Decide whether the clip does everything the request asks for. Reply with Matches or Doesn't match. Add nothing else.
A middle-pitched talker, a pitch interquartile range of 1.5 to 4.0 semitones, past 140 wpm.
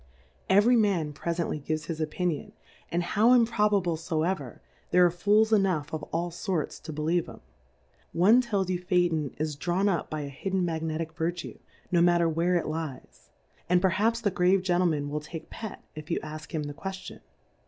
Matches